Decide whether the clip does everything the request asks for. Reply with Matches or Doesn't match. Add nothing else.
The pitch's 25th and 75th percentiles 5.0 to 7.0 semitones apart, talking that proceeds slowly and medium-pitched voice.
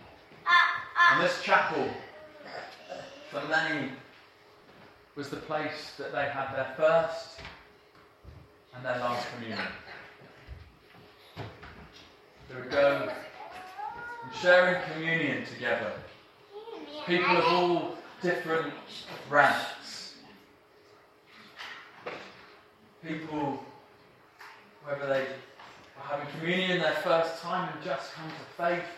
Doesn't match